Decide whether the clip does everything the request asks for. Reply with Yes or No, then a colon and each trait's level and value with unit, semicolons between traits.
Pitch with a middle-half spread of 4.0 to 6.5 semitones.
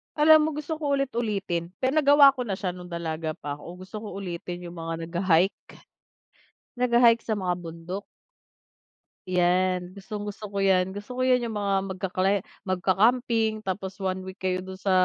Yes: average, 4.3 semitones